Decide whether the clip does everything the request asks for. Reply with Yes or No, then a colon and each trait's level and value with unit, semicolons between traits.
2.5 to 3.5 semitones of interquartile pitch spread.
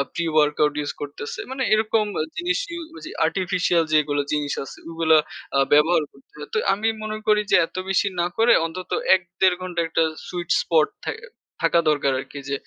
No: average, 4.6 semitones